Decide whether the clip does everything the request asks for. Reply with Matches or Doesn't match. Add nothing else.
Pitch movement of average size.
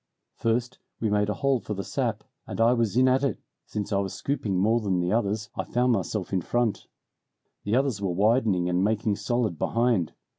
Matches